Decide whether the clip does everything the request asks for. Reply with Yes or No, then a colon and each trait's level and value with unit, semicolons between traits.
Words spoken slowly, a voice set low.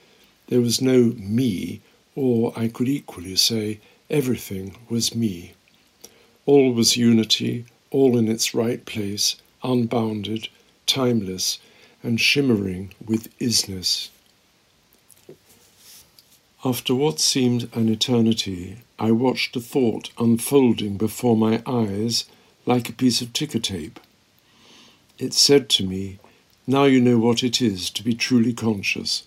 Yes: slow, 120 wpm; low, 115 Hz